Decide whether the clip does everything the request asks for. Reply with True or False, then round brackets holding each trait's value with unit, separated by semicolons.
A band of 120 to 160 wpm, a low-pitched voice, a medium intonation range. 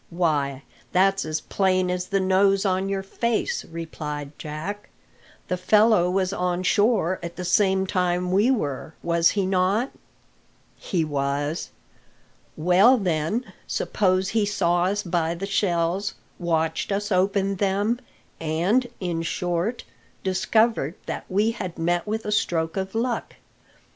False (135 wpm; 185 Hz; 3.1 semitones)